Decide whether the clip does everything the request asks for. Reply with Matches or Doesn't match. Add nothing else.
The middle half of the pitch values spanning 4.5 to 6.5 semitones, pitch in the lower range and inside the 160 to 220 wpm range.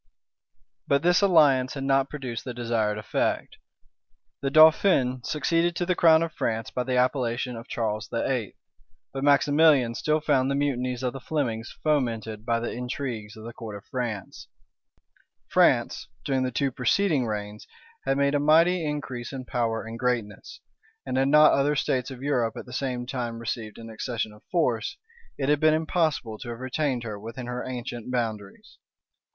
Doesn't match